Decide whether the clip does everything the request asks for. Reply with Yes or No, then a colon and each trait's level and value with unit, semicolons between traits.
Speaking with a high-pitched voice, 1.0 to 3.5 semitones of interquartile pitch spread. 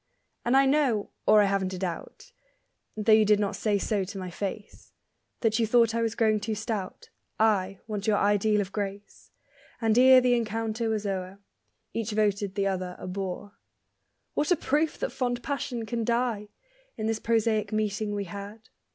Yes: high, 215 Hz; narrow, 2.4 semitones